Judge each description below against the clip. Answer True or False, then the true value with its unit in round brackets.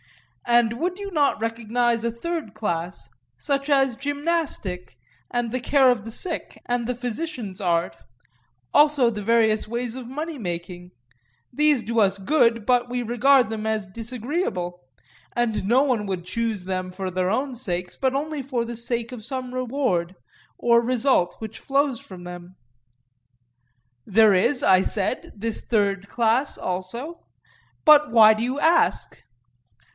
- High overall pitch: True (235 Hz)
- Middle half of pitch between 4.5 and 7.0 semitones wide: True (4.9 semitones)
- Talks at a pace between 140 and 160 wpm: True (150 wpm)